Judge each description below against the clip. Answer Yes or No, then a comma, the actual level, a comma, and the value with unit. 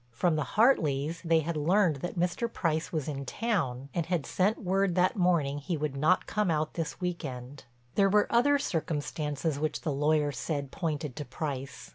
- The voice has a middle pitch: Yes, medium, 155 Hz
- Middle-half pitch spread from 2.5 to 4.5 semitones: Yes, average, 3.9 semitones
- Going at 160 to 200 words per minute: Yes, average, 185 wpm